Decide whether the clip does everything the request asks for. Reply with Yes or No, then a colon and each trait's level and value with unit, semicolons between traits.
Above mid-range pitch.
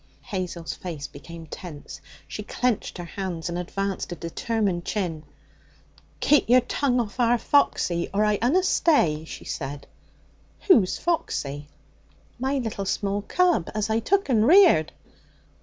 Yes: high, 200 Hz